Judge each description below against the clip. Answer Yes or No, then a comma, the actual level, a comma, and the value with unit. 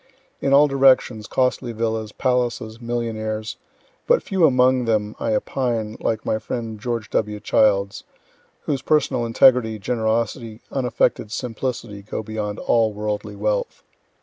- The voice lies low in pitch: Yes, low, 115 Hz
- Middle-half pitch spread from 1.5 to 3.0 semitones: Yes, average, 2.7 semitones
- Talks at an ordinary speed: No, slow, 125 wpm